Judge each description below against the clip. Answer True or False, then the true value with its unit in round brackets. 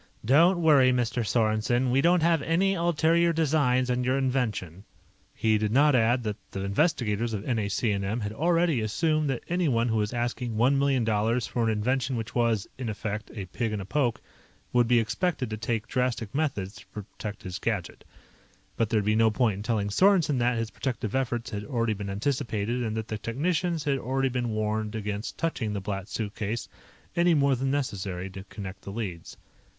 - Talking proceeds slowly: False (190 wpm)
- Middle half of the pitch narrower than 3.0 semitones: False (4.2 semitones)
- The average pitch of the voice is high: False (115 Hz)